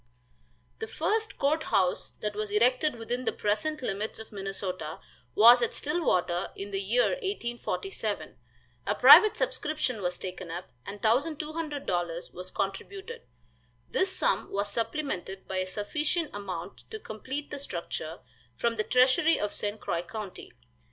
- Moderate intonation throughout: No, wide, 7.5 semitones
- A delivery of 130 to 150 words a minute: Yes, average, 140 wpm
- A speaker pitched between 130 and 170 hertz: No, high, 220 Hz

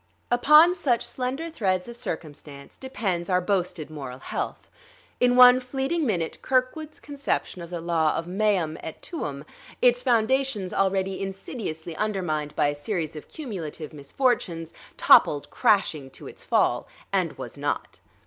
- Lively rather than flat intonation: Yes, wide, 7.7 semitones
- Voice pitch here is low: No, high, 195 Hz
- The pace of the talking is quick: No, average, 140 wpm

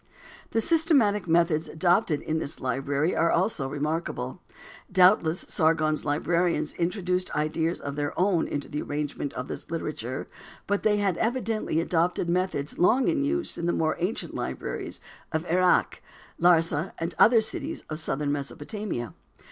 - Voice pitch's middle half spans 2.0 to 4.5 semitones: Yes, average, 4.0 semitones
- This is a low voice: No, medium, 170 Hz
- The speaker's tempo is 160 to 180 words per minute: No, average, 145 wpm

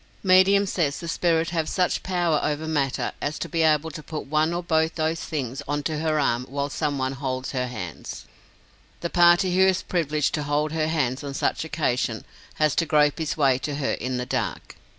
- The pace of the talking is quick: Yes, fast, 210 wpm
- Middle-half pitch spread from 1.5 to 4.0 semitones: Yes, average, 2.8 semitones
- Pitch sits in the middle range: Yes, medium, 155 Hz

